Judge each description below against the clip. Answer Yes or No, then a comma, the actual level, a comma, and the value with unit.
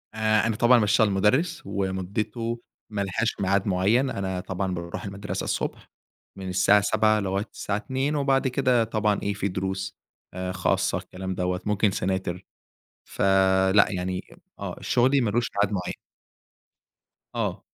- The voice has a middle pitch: No, low, 100 Hz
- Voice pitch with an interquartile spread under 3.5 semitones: Yes, average, 2.9 semitones